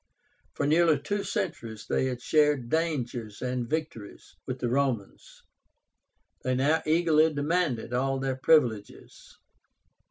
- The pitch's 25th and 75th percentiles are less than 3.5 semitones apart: No, average, 4.4 semitones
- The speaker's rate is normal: No, slow, 120 wpm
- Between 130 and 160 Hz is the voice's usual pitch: Yes, low, 135 Hz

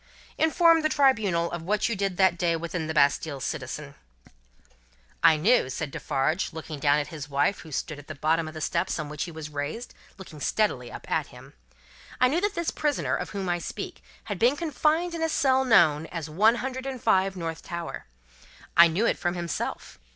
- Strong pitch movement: Yes, wide, 7.5 semitones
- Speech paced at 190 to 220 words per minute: Yes, average, 200 wpm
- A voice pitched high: No, medium, 170 Hz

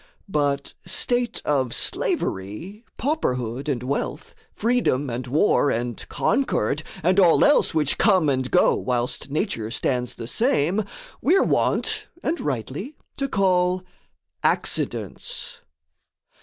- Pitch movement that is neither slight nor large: No, wide, 8.5 semitones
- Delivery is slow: Yes, slow, 115 wpm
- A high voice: No, medium, 150 Hz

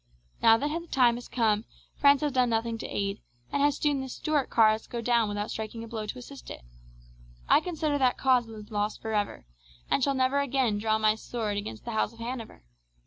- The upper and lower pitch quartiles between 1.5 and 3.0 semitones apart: No, average, 3.6 semitones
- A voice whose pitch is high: Yes, high, 235 Hz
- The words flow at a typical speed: No, fast, 215 wpm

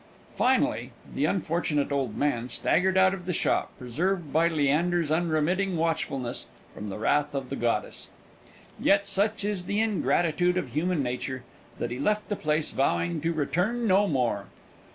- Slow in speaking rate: No, average, 155 wpm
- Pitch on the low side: No, medium, 160 Hz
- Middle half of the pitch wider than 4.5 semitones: Yes, average, 5.3 semitones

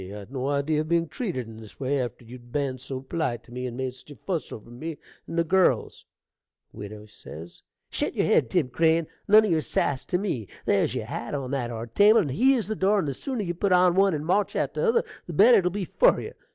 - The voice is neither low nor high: Yes, medium, 150 Hz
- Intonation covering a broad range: Yes, wide, 7.0 semitones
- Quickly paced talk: Yes, fast, 245 wpm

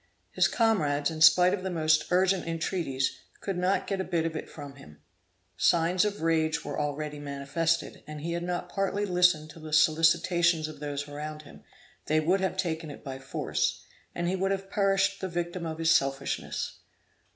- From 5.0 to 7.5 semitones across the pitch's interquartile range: No, average, 3.1 semitones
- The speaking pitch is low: No, medium, 165 Hz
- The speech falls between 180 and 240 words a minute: Yes, average, 185 wpm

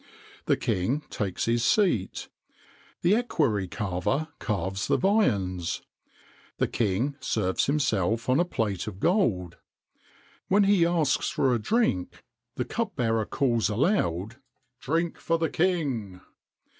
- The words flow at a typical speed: No, slow, 120 wpm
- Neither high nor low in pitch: No, low, 120 Hz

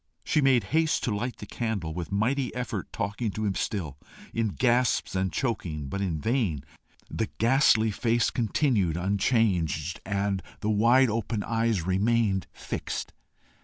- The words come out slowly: No, average, 145 wpm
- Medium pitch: No, low, 110 Hz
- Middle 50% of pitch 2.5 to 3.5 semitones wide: No, average, 3.9 semitones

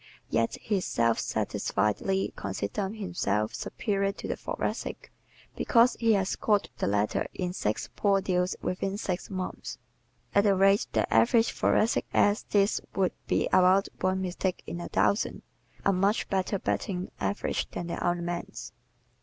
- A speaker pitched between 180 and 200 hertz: Yes, high, 190 Hz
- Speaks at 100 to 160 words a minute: Yes, average, 150 wpm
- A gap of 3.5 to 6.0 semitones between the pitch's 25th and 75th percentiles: No, narrow, 2.4 semitones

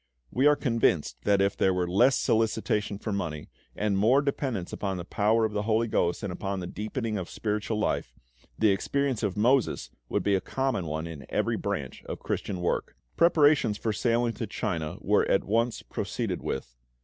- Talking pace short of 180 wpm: No, average, 185 wpm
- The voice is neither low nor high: No, low, 105 Hz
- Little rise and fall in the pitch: No, average, 3.5 semitones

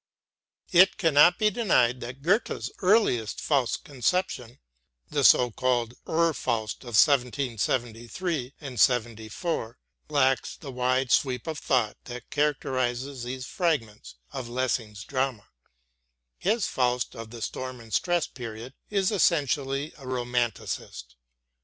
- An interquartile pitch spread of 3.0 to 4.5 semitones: Yes, average, 3.9 semitones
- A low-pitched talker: Yes, low, 130 Hz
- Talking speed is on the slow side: Yes, slow, 120 wpm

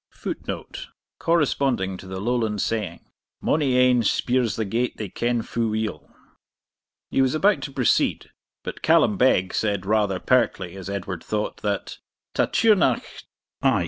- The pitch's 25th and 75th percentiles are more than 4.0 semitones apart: Yes, average, 4.4 semitones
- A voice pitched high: No, low, 110 Hz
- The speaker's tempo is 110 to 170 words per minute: Yes, average, 145 wpm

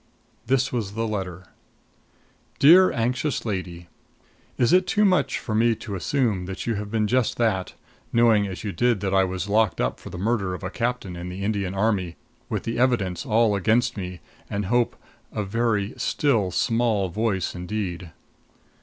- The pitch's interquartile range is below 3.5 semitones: No, average, 3.9 semitones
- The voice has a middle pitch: No, low, 105 Hz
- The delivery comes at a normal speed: Yes, average, 170 wpm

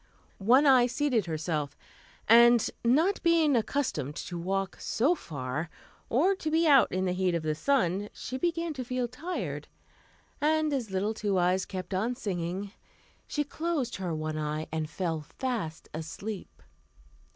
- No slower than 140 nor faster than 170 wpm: Yes, average, 150 wpm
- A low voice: No, high, 210 Hz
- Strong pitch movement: Yes, wide, 8.2 semitones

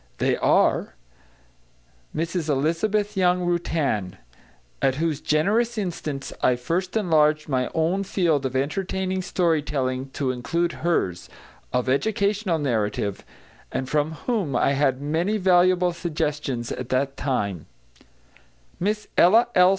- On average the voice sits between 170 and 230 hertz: No, medium, 160 Hz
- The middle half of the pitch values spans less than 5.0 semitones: No, average, 5.3 semitones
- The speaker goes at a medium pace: No, slow, 120 wpm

